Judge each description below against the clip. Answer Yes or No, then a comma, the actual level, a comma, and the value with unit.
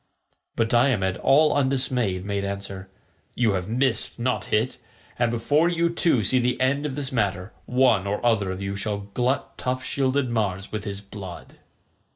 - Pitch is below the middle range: Yes, low, 115 Hz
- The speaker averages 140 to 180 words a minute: Yes, average, 170 wpm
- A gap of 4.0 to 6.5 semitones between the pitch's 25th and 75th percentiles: Yes, average, 4.6 semitones